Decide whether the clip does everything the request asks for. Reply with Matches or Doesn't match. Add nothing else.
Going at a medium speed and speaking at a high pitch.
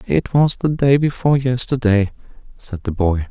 Doesn't match